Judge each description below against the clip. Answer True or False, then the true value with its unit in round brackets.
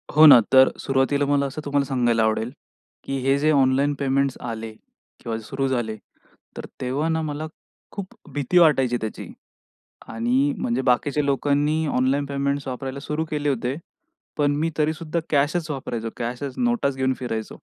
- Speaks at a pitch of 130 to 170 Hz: True (140 Hz)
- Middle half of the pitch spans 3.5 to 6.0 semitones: False (2.6 semitones)